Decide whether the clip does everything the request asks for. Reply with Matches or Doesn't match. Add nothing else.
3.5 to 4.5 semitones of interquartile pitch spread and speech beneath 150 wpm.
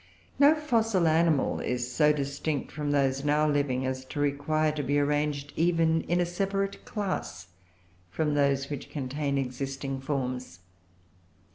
Doesn't match